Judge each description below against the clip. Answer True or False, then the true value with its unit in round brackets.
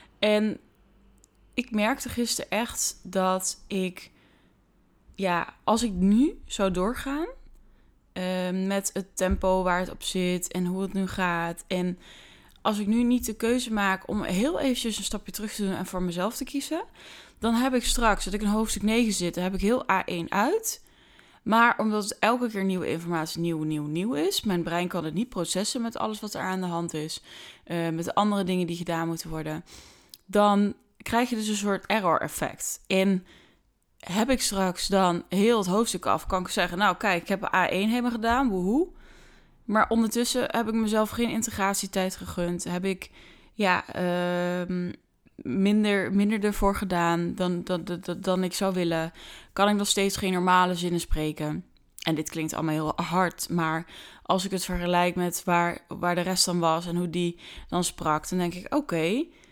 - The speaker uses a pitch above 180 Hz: True (190 Hz)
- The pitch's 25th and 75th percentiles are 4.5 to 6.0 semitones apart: False (3.5 semitones)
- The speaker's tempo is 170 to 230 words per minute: True (185 wpm)